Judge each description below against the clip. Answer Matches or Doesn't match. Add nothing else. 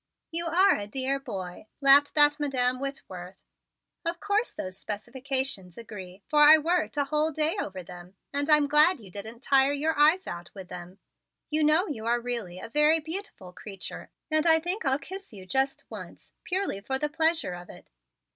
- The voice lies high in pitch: Matches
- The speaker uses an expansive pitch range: Matches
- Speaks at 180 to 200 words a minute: Matches